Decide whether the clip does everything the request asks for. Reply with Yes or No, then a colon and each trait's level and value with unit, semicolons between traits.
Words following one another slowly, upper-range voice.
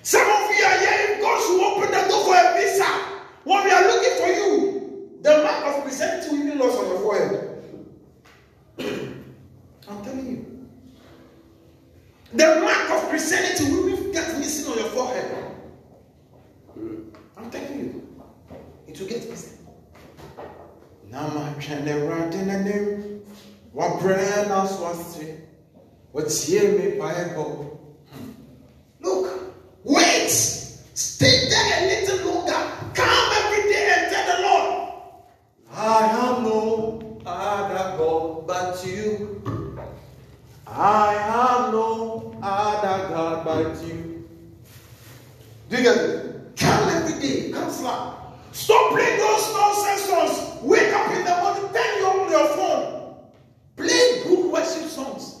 Yes: slow, 120 wpm; very high, 270 Hz